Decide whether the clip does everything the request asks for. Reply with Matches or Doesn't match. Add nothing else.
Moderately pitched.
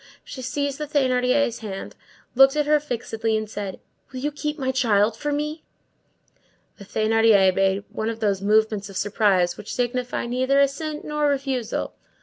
Doesn't match